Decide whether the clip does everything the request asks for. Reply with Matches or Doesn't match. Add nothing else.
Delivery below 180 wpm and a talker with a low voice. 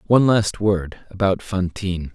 Matches